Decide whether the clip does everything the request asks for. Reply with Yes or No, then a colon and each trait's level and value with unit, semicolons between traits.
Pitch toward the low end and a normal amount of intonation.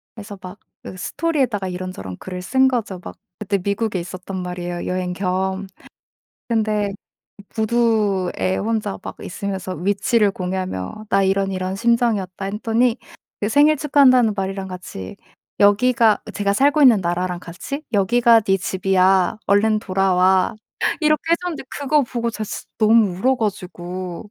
No: high, 200 Hz; average, 3.8 semitones